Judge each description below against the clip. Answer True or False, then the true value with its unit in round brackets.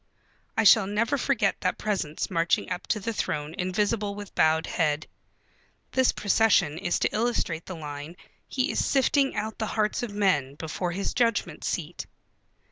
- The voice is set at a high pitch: True (200 Hz)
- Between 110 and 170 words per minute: True (160 wpm)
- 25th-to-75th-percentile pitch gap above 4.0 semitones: True (5.1 semitones)